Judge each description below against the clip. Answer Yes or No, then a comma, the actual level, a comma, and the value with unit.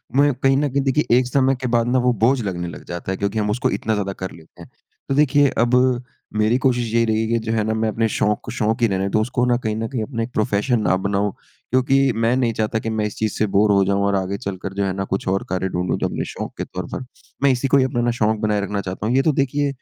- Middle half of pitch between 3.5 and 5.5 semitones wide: Yes, average, 3.9 semitones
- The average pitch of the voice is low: Yes, low, 110 Hz